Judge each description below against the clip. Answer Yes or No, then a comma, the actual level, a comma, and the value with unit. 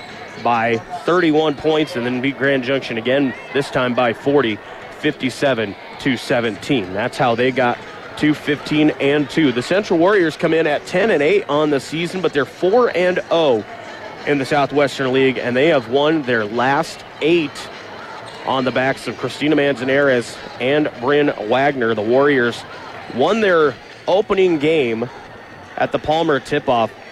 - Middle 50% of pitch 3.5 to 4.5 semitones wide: No, average, 3.1 semitones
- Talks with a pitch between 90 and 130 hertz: No, medium, 140 Hz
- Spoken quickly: No, average, 160 wpm